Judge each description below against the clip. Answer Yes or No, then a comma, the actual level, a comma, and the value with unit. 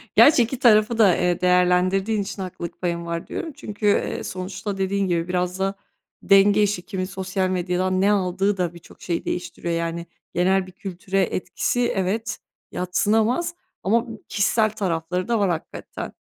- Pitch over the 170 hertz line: Yes, high, 190 Hz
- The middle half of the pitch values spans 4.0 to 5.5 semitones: No, narrow, 2.5 semitones